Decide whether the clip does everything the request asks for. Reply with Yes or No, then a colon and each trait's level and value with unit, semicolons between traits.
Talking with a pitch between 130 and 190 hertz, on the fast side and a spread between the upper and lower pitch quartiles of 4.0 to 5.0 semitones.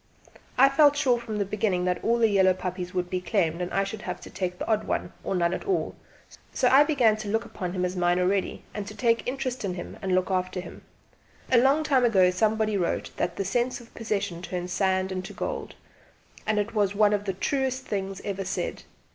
No: high, 200 Hz; fast, 230 wpm; average, 4.3 semitones